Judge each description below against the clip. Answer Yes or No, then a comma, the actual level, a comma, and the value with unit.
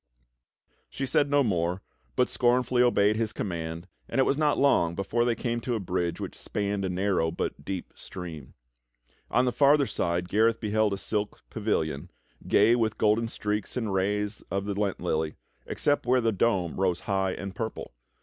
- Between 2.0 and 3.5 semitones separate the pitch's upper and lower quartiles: No, average, 4.3 semitones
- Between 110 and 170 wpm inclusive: No, average, 180 wpm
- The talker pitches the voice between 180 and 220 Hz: No, low, 105 Hz